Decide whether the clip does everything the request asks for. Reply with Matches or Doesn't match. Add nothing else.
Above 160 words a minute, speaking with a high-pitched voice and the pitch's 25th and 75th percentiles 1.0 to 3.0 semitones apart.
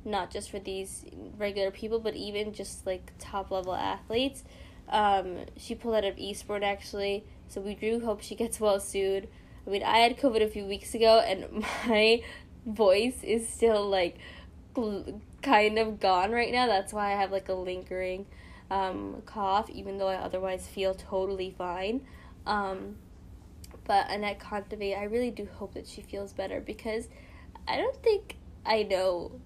Matches